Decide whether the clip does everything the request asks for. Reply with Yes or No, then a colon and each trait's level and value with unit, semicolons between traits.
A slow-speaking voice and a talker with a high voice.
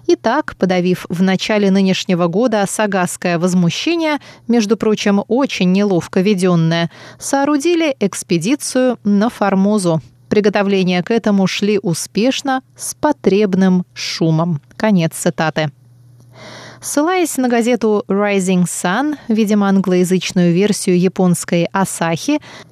Yes: slow, 100 wpm; high, 195 Hz